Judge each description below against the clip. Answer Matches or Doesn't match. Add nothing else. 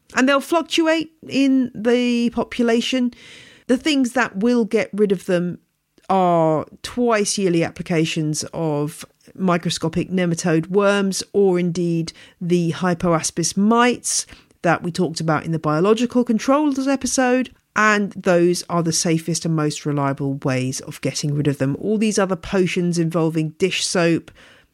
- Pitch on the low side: Doesn't match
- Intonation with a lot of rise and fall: Matches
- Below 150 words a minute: Matches